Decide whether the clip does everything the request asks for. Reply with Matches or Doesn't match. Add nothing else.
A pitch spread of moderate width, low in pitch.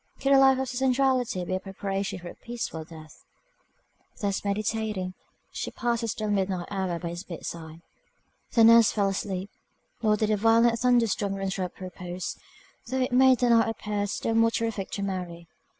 Doesn't match